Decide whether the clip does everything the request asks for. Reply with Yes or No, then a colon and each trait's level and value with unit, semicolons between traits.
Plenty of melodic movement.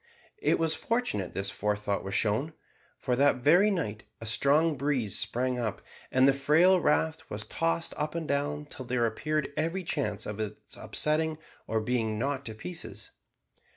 Yes: wide, 6.1 semitones